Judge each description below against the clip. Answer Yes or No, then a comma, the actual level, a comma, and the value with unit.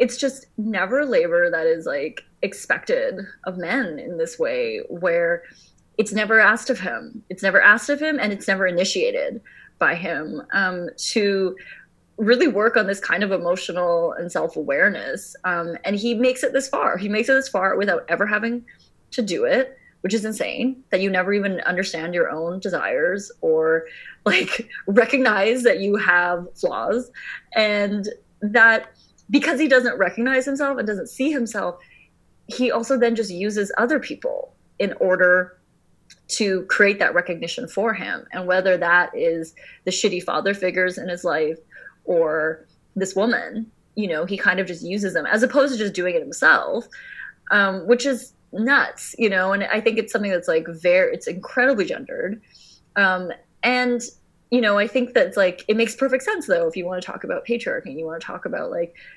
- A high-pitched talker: Yes, high, 220 Hz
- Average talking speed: Yes, average, 180 wpm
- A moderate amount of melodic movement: No, wide, 6.3 semitones